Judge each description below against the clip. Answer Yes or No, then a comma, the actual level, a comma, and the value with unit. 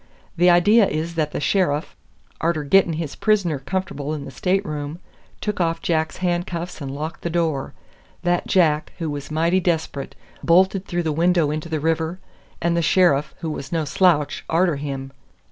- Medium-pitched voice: Yes, medium, 165 Hz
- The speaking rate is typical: Yes, average, 170 wpm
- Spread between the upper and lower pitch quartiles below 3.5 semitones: Yes, average, 2.8 semitones